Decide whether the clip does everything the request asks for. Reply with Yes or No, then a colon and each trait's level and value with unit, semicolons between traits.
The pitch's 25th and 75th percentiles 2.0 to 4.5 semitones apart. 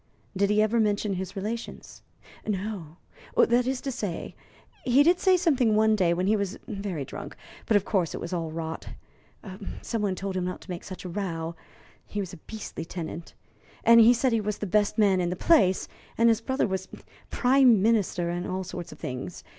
Yes: average, 4.1 semitones